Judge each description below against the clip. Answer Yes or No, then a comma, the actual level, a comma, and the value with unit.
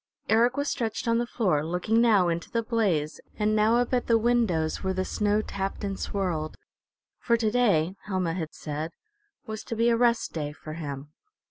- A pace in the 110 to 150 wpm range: No, average, 195 wpm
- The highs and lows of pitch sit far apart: Yes, wide, 5.7 semitones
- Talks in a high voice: Yes, high, 205 Hz